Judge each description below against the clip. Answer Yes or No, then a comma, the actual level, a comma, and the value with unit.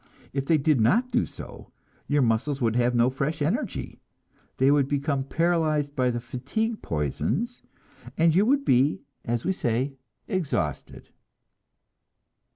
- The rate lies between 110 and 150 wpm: Yes, average, 140 wpm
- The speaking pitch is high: No, medium, 140 Hz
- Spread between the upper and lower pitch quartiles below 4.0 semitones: No, average, 5.0 semitones